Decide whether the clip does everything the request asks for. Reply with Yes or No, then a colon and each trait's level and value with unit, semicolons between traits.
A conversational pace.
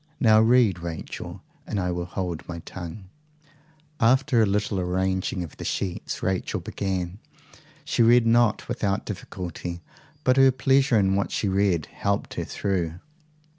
Yes: average, 145 wpm